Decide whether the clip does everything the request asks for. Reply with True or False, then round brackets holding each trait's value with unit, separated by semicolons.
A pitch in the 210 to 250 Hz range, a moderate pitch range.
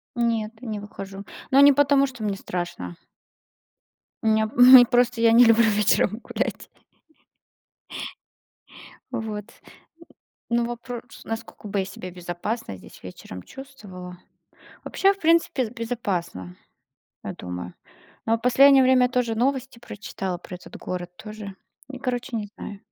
True (225 Hz; 4.2 semitones)